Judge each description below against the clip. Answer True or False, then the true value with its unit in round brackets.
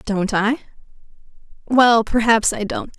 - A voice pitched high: True (220 Hz)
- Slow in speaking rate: True (120 wpm)